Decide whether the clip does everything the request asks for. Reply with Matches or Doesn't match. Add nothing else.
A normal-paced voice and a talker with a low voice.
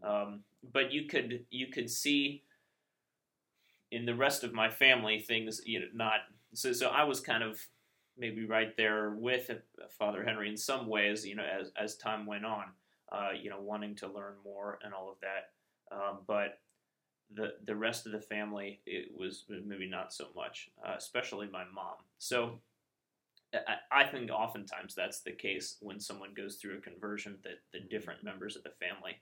Matches